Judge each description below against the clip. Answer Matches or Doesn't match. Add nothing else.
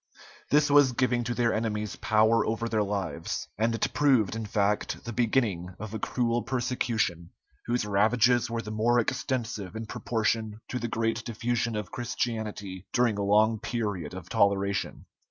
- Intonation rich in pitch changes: Doesn't match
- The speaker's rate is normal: Matches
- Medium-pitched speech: Doesn't match